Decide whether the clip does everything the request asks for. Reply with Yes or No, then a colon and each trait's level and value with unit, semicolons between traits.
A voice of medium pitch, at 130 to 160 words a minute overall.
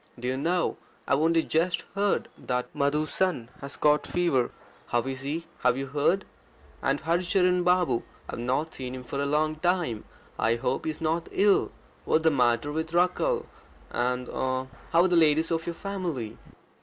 No: medium, 155 Hz; average, 185 wpm